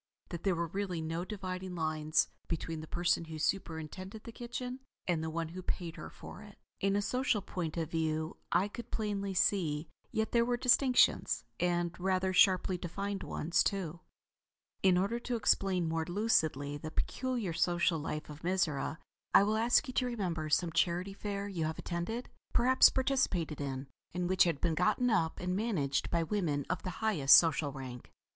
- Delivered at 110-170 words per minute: No, average, 180 wpm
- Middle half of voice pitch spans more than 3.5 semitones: Yes, average, 4.2 semitones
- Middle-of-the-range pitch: Yes, medium, 180 Hz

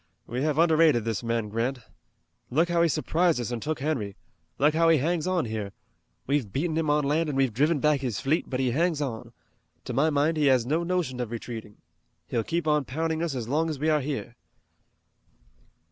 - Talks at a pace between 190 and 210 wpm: Yes, fast, 205 wpm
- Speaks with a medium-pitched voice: Yes, medium, 145 Hz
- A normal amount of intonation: Yes, average, 4.7 semitones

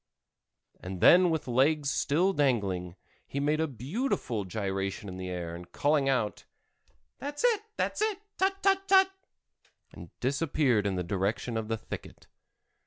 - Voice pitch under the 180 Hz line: Yes, low, 135 Hz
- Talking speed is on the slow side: Yes, slow, 125 wpm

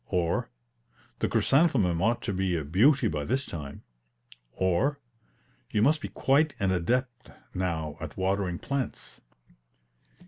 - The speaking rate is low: Yes, slow, 130 wpm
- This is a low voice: Yes, very low, 95 Hz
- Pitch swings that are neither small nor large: No, wide, 7.3 semitones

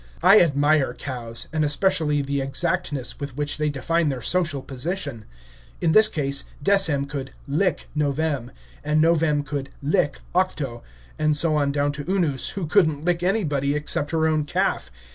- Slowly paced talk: No, average, 160 wpm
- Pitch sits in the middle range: Yes, medium, 150 Hz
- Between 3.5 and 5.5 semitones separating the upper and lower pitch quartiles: No, average, 3.0 semitones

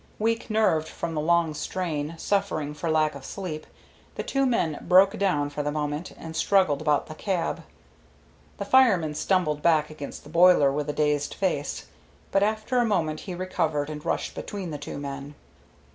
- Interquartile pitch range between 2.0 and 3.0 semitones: No, average, 4.2 semitones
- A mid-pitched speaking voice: Yes, medium, 160 Hz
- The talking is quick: No, average, 175 wpm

